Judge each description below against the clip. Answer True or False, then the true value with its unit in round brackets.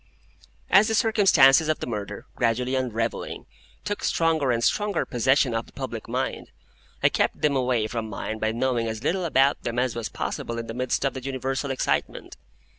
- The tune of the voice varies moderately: True (3.7 semitones)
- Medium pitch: False (130 Hz)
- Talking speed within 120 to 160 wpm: False (185 wpm)